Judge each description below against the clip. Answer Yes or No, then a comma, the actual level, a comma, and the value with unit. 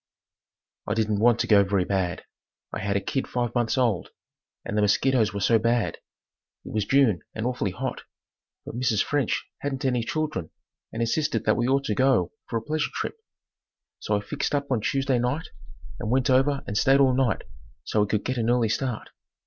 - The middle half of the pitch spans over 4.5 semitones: No, average, 4.1 semitones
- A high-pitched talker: No, low, 120 Hz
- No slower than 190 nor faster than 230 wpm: Yes, average, 195 wpm